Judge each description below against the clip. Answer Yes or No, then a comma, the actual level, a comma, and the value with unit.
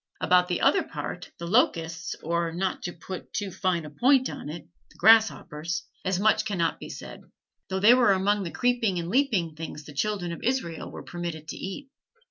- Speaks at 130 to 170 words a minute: No, average, 195 wpm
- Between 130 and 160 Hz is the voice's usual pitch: No, medium, 180 Hz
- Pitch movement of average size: Yes, average, 4.2 semitones